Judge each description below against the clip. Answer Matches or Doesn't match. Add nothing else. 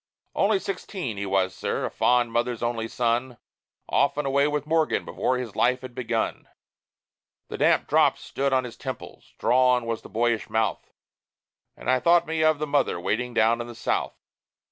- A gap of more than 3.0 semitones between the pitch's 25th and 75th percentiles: Matches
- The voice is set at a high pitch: Doesn't match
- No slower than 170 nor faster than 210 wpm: Matches